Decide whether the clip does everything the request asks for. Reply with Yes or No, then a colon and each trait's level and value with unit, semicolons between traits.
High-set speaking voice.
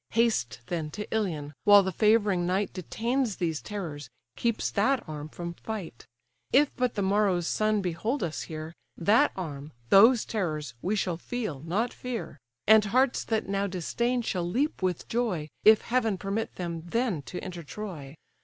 Yes: high, 195 Hz